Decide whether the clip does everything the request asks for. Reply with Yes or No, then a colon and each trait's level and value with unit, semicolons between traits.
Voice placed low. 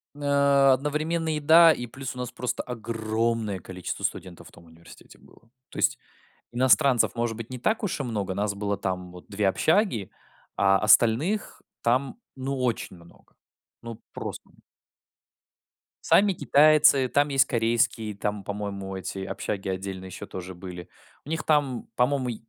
Yes: low, 115 Hz